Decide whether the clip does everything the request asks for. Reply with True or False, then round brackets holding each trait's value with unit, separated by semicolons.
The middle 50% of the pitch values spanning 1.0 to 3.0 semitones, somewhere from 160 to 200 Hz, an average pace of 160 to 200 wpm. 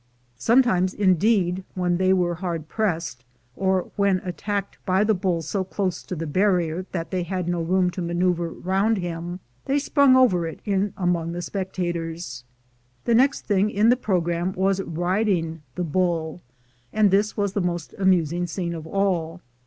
True (2.5 semitones; 185 Hz; 165 wpm)